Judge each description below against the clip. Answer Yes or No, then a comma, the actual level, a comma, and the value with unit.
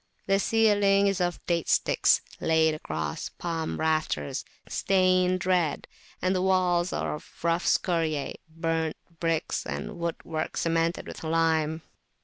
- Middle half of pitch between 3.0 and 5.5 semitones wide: No, narrow, 2.5 semitones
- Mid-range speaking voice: Yes, medium, 165 Hz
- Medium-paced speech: No, slow, 130 wpm